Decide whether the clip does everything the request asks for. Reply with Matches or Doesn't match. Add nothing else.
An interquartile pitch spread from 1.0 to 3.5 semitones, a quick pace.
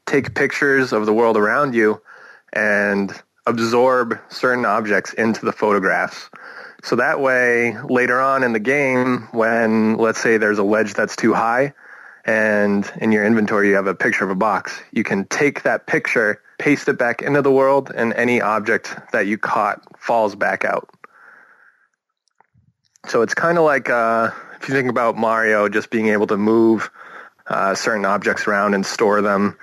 Doesn't match